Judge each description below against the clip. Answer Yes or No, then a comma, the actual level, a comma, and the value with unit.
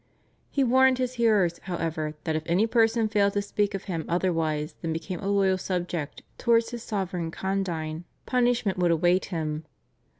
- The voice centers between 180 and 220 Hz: Yes, high, 190 Hz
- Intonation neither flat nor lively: Yes, average, 5.0 semitones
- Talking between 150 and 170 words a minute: Yes, average, 165 wpm